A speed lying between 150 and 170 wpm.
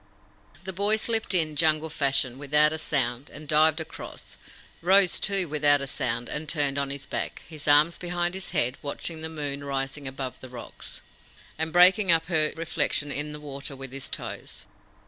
No: average, 180 wpm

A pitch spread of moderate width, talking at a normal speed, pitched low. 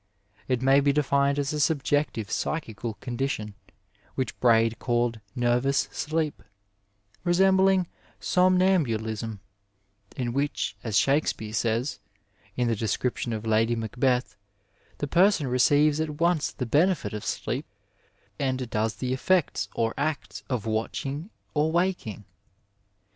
No: average, 5.0 semitones; slow, 120 wpm; low, 130 Hz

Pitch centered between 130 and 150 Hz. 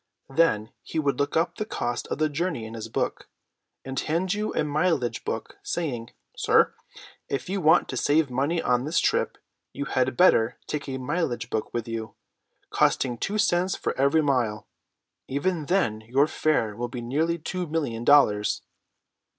Yes: medium, 140 Hz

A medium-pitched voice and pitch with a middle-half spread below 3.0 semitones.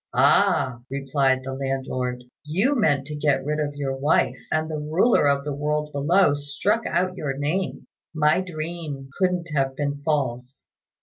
Yes: medium, 145 Hz; narrow, 2.5 semitones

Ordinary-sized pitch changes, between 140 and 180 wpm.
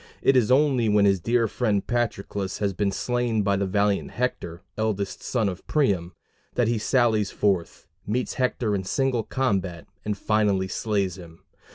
Yes: average, 3.7 semitones; average, 165 wpm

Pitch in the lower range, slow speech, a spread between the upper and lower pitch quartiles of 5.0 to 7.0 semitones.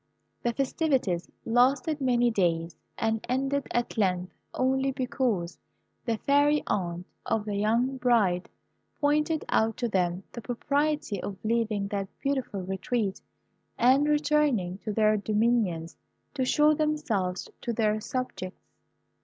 No: high, 230 Hz; slow, 125 wpm; average, 5.3 semitones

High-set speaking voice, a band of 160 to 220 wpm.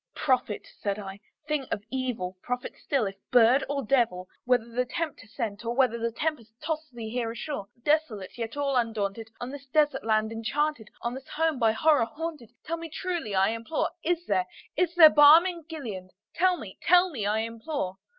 Yes: very high, 250 Hz; average, 180 wpm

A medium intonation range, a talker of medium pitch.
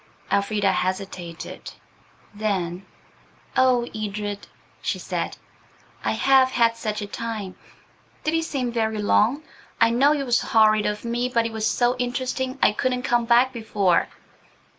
No: average, 3.3 semitones; high, 230 Hz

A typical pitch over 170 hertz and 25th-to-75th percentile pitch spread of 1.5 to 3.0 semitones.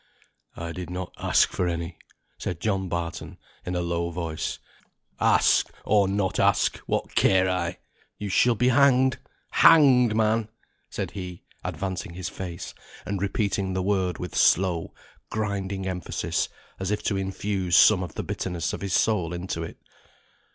No: very low, 95 Hz; average, 2.7 semitones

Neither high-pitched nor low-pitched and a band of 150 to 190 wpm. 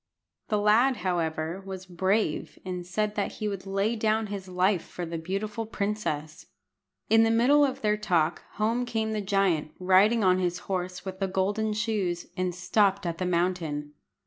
No: high, 195 Hz; average, 170 wpm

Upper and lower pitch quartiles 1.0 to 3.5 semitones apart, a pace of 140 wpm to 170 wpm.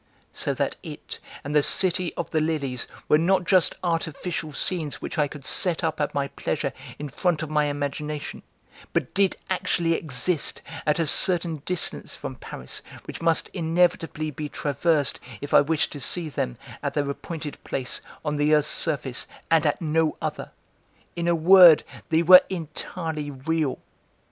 Yes: narrow, 2.6 semitones; average, 165 wpm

